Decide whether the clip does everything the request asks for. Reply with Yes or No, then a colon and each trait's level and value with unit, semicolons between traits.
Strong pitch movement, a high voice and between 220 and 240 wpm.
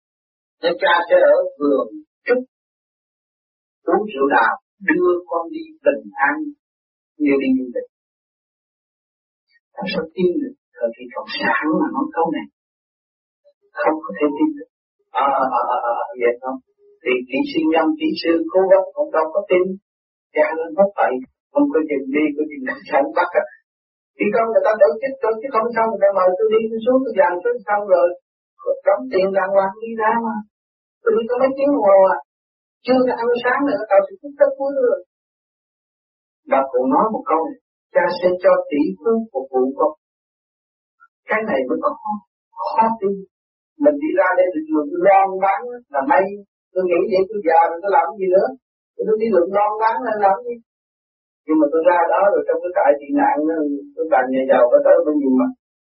No: wide, 8.2 semitones; high, 220 Hz; average, 205 wpm